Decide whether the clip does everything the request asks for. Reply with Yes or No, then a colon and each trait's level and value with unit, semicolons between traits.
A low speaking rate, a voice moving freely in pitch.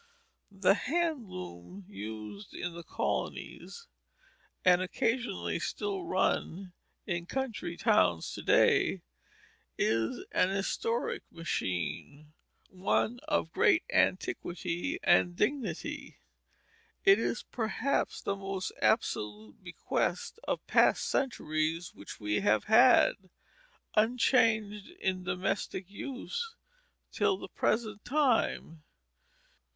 Yes: slow, 95 wpm; wide, 6.7 semitones